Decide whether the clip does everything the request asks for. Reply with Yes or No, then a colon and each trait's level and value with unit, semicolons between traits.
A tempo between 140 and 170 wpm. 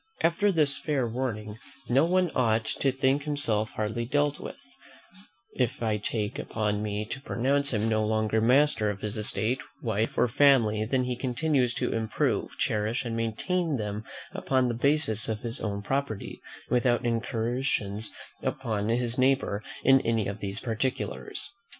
Yes: average, 155 wpm